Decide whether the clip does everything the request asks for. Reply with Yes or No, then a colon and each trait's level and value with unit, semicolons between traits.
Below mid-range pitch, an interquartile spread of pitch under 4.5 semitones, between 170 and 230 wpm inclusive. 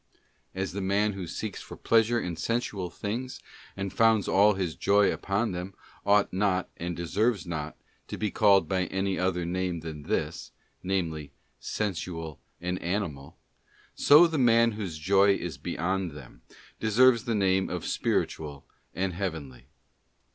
No: very low, 95 Hz; average, 3.4 semitones; average, 145 wpm